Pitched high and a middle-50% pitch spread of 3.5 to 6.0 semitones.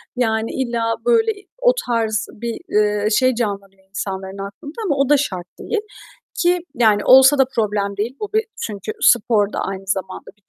Yes: high, 225 Hz; average, 4.8 semitones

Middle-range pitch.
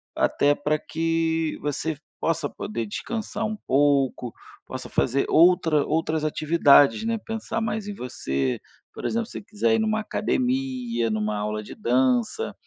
Yes: medium, 165 Hz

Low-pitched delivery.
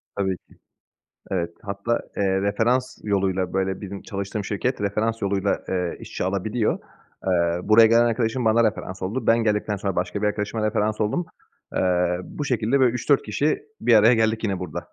Yes: low, 105 Hz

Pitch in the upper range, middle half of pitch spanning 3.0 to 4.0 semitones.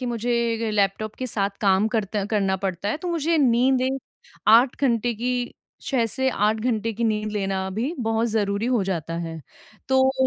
Yes: high, 225 Hz; average, 3.7 semitones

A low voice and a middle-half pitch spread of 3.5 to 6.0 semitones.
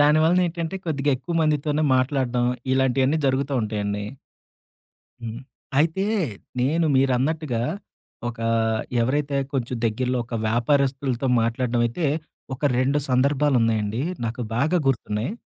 Yes: low, 130 Hz; average, 3.8 semitones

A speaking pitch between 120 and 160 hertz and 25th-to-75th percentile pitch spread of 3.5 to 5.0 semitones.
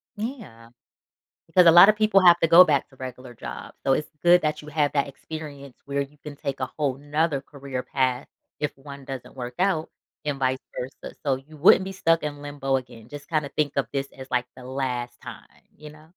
No: medium, 140 Hz; average, 2.9 semitones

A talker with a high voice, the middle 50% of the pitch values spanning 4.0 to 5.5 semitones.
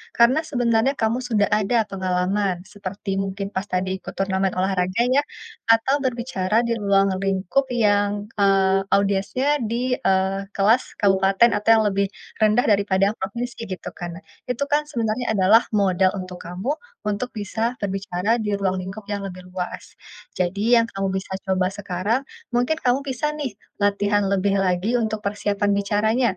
No: high, 205 Hz; average, 3.2 semitones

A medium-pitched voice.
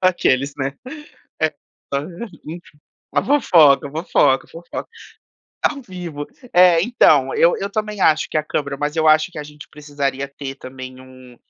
Yes: medium, 150 Hz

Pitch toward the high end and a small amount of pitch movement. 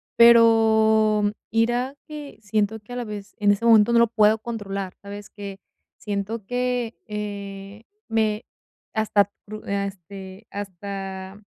Yes: high, 210 Hz; narrow, 2.2 semitones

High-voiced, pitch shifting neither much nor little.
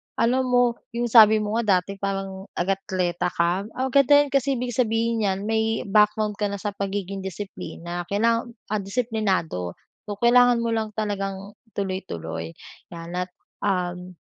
Yes: high, 205 Hz; average, 3.2 semitones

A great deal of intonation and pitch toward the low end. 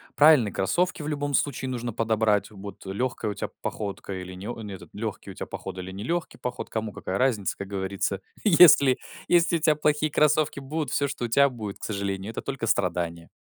Yes: wide, 6.4 semitones; low, 115 Hz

